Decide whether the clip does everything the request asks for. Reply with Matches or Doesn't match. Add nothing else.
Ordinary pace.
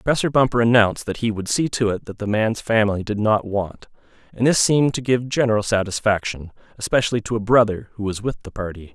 Doesn't match